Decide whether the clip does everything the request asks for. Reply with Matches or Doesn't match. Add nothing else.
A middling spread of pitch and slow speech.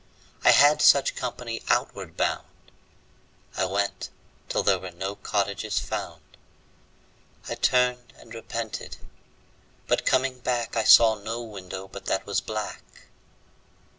Matches